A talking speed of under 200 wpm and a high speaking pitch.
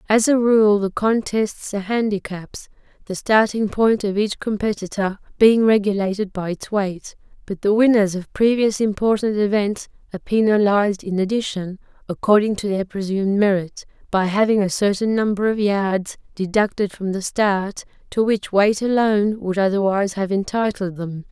Yes: average, 150 wpm; high, 205 Hz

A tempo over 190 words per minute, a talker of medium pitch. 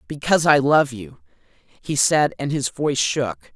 No: average, 170 wpm; medium, 145 Hz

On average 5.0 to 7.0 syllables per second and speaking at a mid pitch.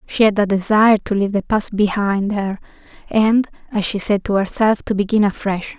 No: 5.4 syllables/s; high, 205 Hz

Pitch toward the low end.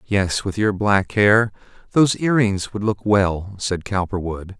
Yes: low, 100 Hz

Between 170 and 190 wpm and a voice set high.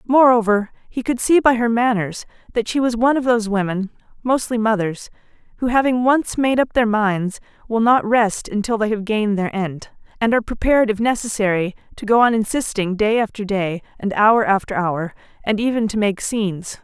Yes: average, 185 wpm; high, 220 Hz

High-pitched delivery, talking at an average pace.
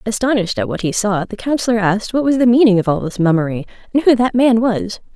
No: high, 220 Hz; fast, 245 wpm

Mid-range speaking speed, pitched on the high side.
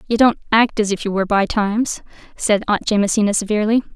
Yes: average, 195 wpm; high, 210 Hz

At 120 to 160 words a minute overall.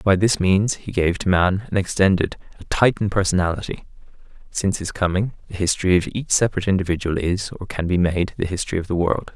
No: average, 200 wpm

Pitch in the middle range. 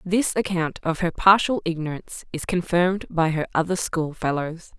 Yes: medium, 170 Hz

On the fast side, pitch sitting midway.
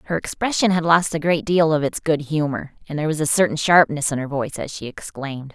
Yes: fast, 250 wpm; medium, 155 Hz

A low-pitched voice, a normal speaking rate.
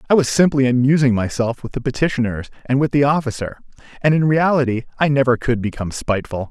Yes: low, 130 Hz; average, 185 wpm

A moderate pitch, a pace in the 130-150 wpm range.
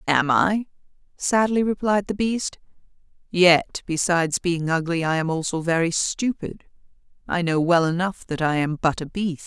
No: medium, 175 Hz; average, 160 wpm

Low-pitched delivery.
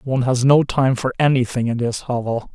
Yes: low, 125 Hz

